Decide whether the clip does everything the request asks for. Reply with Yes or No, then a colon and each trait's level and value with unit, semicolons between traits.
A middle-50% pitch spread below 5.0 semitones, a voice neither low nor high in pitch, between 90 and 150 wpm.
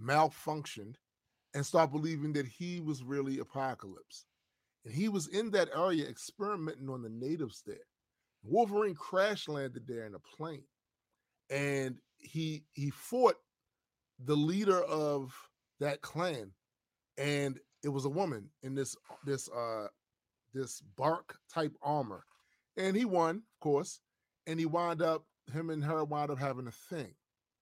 Yes: average, 3.7 semitones; medium, 145 Hz; average, 145 wpm